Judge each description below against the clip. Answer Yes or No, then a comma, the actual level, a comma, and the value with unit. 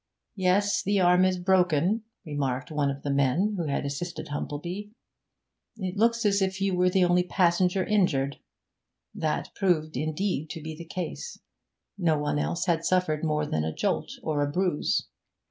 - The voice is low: No, medium, 175 Hz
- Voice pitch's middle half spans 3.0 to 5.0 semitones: Yes, average, 4.1 semitones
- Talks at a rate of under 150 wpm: No, average, 165 wpm